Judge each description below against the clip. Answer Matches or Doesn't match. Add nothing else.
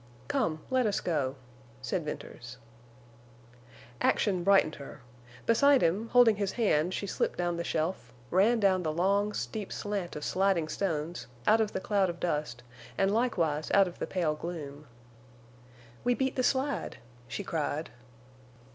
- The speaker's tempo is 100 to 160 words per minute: Matches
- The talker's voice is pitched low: Doesn't match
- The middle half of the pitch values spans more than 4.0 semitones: Matches